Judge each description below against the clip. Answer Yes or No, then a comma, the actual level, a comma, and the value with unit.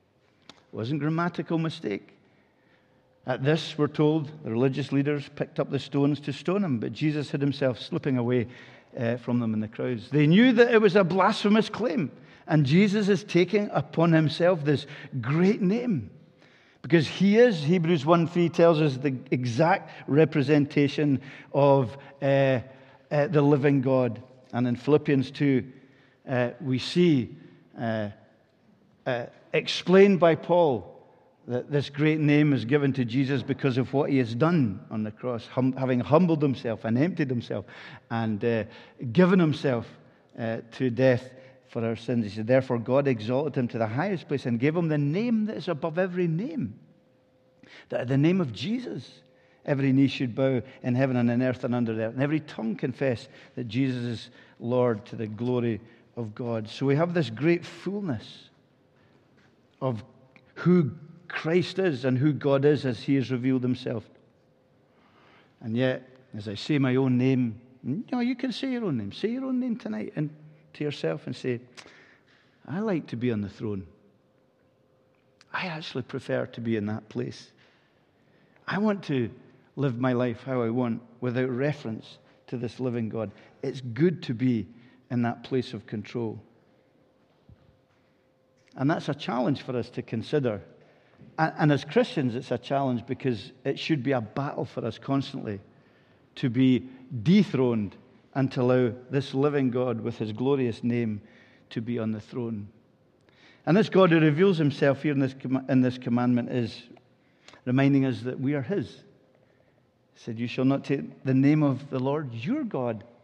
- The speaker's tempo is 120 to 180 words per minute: Yes, average, 170 wpm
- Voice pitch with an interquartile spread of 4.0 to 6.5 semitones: No, average, 3.6 semitones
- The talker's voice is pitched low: Yes, low, 130 Hz